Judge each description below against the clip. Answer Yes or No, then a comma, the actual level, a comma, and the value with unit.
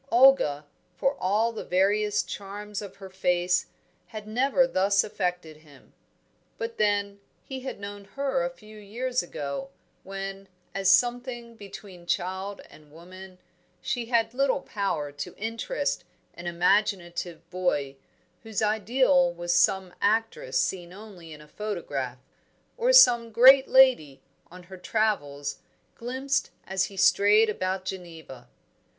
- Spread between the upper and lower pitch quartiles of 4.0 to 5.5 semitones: Yes, average, 4.6 semitones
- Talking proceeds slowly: Yes, slow, 130 wpm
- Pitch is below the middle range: No, high, 200 Hz